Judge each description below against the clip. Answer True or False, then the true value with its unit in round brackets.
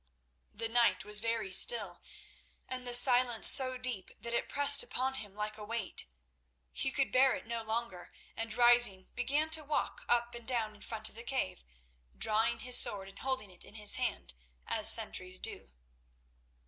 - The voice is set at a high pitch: True (230 Hz)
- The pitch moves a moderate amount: True (3.1 semitones)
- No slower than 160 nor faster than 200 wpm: True (175 wpm)